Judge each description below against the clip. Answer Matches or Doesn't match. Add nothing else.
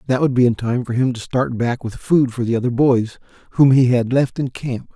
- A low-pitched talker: Matches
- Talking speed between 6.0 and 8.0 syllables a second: Doesn't match